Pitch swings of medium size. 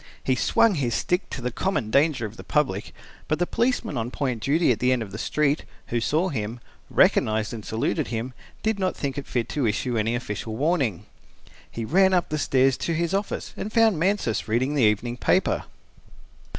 No: wide, 6.5 semitones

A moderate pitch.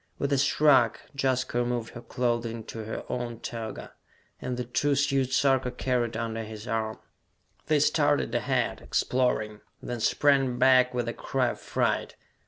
No: low, 125 Hz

